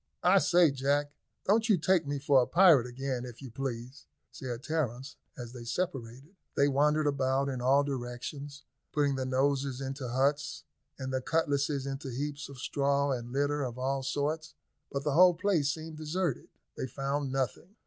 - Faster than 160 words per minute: Yes, average, 170 wpm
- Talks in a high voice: No, medium, 140 Hz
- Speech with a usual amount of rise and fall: No, narrow, 2.3 semitones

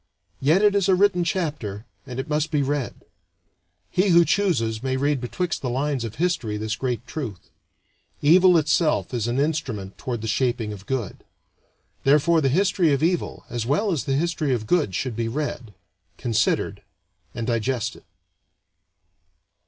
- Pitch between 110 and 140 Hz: Yes, low, 135 Hz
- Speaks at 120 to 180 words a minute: Yes, average, 160 wpm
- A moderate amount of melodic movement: No, wide, 6.0 semitones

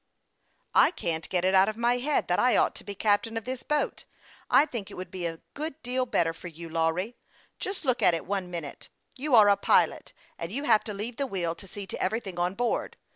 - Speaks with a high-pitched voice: Yes, high, 205 Hz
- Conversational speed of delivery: No, fast, 240 wpm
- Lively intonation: Yes, wide, 5.7 semitones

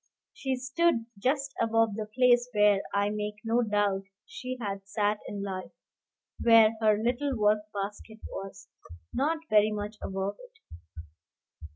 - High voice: Yes, high, 215 Hz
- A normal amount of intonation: Yes, average, 3.2 semitones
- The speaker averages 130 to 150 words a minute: Yes, average, 140 wpm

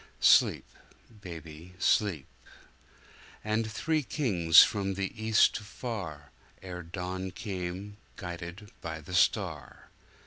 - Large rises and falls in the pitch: No, average, 3.7 semitones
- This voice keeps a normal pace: No, slow, 90 wpm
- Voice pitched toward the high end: No, very low, 95 Hz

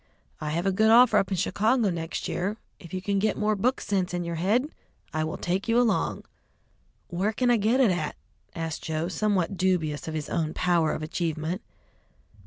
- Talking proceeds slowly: No, average, 195 wpm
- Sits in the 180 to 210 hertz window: Yes, medium, 185 Hz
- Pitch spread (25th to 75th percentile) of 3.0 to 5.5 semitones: Yes, average, 4.5 semitones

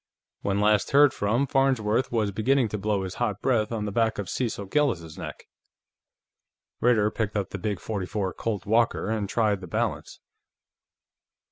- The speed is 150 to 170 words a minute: Yes, average, 160 wpm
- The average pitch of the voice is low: Yes, low, 105 Hz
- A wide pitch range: No, average, 2.7 semitones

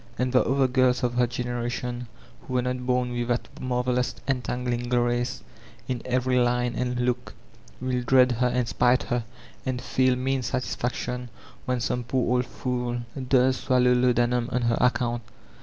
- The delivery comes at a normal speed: Yes, average, 155 wpm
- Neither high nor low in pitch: No, low, 125 Hz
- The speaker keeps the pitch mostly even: Yes, narrow, 0.7 semitones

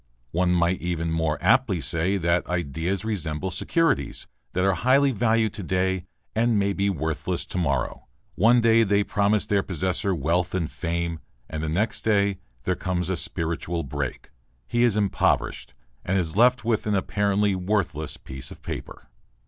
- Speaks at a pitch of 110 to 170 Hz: No, very low, 95 Hz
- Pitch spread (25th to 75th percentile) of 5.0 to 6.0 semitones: No, average, 3.7 semitones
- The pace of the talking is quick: No, average, 165 wpm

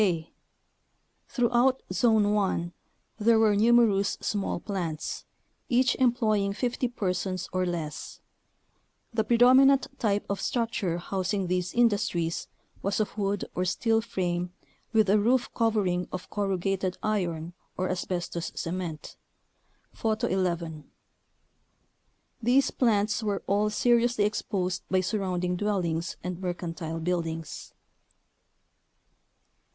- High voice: Yes, high, 195 Hz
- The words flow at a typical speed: No, slow, 110 wpm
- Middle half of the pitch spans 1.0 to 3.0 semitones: No, average, 3.8 semitones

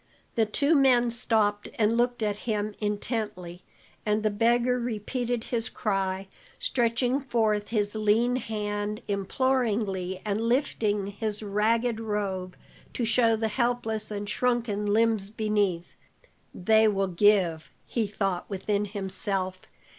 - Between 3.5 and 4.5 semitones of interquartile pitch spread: No, narrow, 2.4 semitones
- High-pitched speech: Yes, high, 215 Hz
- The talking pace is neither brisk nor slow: No, slow, 125 wpm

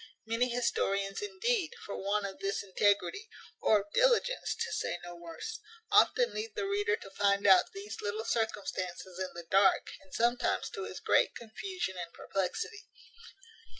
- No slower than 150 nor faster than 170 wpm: Yes, average, 155 wpm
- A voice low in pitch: No, high, 205 Hz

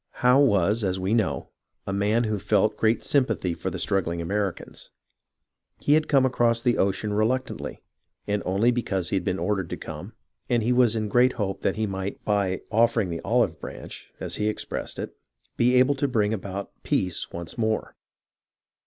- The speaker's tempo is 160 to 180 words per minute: No, average, 190 wpm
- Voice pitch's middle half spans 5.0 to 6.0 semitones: No, average, 3.5 semitones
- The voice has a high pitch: No, low, 105 Hz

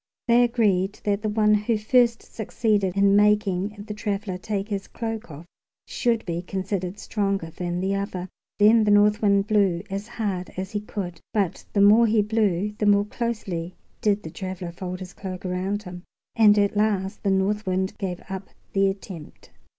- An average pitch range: No, narrow, 2.1 semitones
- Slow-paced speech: No, average, 180 wpm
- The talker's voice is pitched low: No, high, 200 Hz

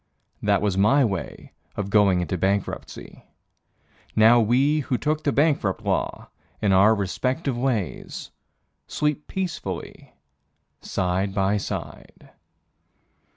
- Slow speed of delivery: Yes, slow, 110 wpm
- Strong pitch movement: Yes, wide, 5.8 semitones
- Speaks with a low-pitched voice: Yes, low, 105 Hz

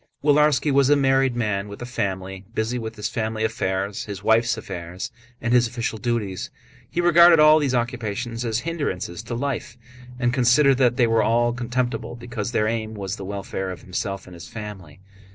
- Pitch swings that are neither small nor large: Yes, average, 3.7 semitones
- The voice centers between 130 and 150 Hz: No, low, 115 Hz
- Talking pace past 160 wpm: Yes, average, 185 wpm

